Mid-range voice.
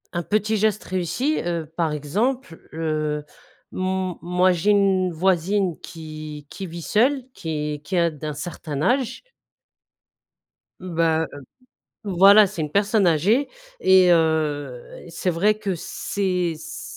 Yes: medium, 175 Hz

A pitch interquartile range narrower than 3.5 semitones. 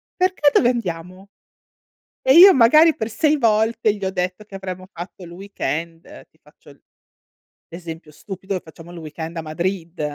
No: average, 5.0 semitones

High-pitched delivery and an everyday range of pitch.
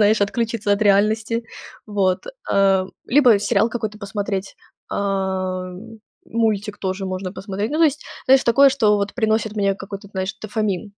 No: high, 205 Hz; narrow, 2.3 semitones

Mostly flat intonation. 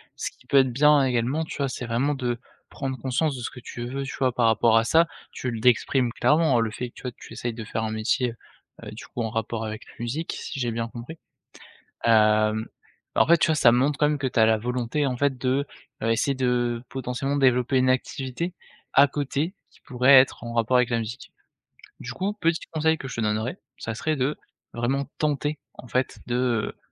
No: average, 3.0 semitones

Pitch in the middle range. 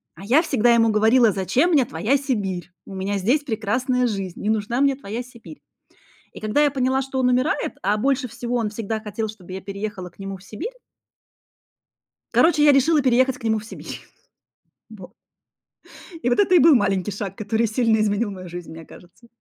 No: high, 225 Hz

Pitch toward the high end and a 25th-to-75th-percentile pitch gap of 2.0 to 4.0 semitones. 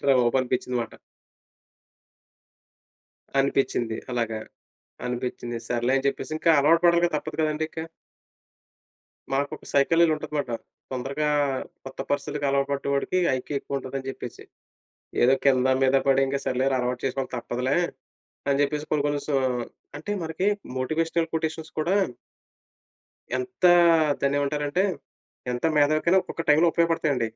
No: medium, 140 Hz; average, 3.2 semitones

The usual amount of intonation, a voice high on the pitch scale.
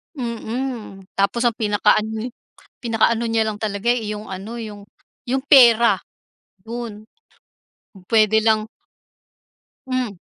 No: narrow, 2.1 semitones; high, 220 Hz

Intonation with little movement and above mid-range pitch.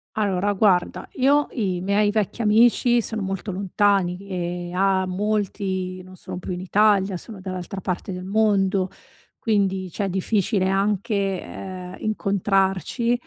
Yes: narrow, 2.3 semitones; high, 195 Hz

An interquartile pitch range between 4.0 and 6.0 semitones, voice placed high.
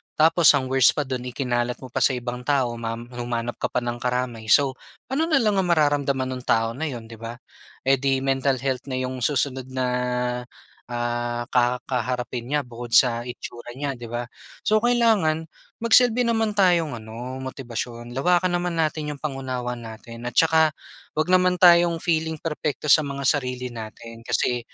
No: average, 4.4 semitones; low, 130 Hz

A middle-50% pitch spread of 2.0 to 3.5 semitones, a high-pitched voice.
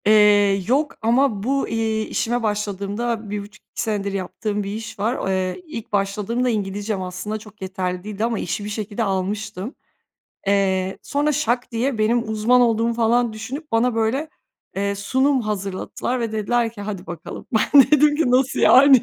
Yes: average, 3.2 semitones; high, 220 Hz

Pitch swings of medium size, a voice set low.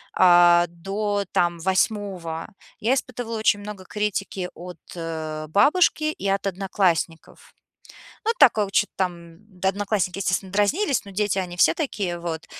No: average, 3.2 semitones; high, 195 Hz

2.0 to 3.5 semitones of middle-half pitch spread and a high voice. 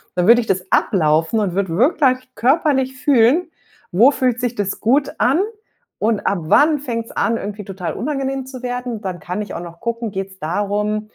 No: average, 5.0 semitones; high, 230 Hz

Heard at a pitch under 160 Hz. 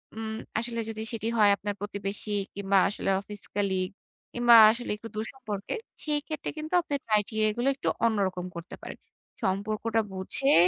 No: high, 215 Hz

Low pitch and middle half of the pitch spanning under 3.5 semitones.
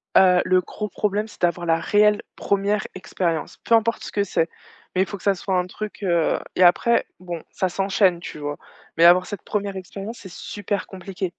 No: high, 190 Hz; narrow, 2.6 semitones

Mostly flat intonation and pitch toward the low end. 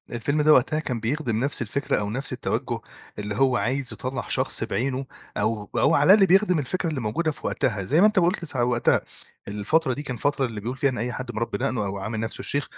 No: average, 4.6 semitones; low, 130 Hz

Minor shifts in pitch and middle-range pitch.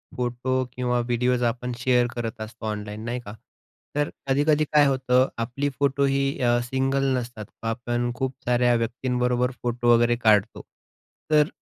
No: narrow, 1.8 semitones; low, 125 Hz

